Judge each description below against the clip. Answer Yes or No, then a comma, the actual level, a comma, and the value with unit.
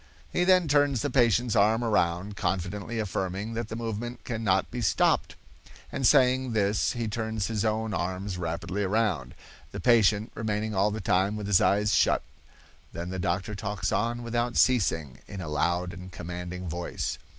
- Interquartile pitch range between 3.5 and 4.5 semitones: Yes, average, 3.9 semitones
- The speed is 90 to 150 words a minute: No, average, 165 wpm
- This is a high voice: No, low, 105 Hz